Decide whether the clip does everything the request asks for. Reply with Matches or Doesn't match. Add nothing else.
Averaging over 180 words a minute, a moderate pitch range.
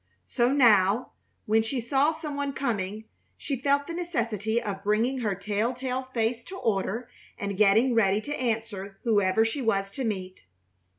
Doesn't match